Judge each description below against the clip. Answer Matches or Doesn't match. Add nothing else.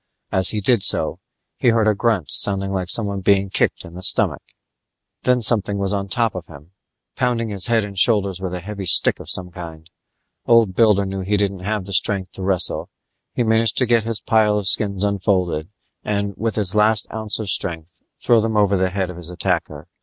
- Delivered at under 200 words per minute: Doesn't match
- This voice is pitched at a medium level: Doesn't match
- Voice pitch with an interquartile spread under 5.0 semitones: Matches